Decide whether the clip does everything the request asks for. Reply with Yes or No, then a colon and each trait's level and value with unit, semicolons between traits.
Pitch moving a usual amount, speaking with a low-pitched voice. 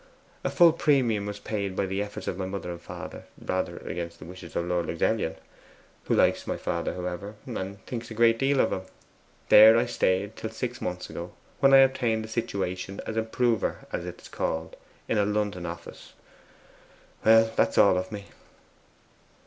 Yes: average, 3.8 semitones; low, 100 Hz